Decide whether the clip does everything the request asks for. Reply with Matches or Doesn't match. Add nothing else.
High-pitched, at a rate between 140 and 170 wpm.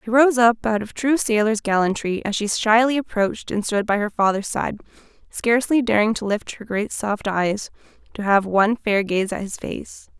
Doesn't match